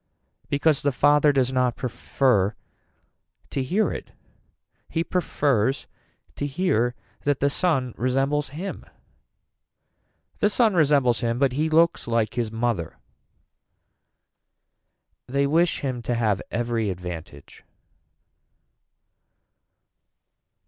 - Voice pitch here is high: No, low, 130 Hz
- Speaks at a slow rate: Yes, slow, 100 wpm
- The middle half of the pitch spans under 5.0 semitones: Yes, average, 4.0 semitones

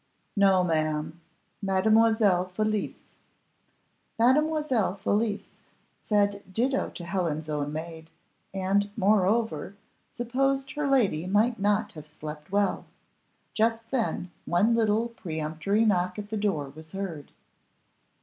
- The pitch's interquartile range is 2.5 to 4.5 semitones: No, average, 4.9 semitones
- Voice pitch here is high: Yes, high, 200 Hz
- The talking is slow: Yes, slow, 110 wpm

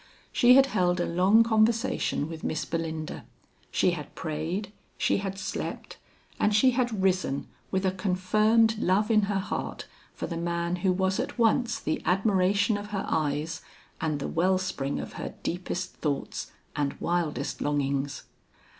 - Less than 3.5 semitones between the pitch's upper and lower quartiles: No, average, 4.2 semitones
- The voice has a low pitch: No, medium, 185 Hz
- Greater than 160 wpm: No, average, 155 wpm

